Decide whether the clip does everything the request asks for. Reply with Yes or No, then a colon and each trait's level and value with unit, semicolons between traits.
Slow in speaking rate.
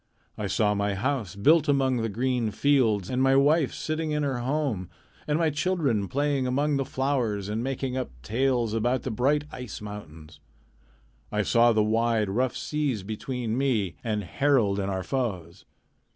No: average, 165 wpm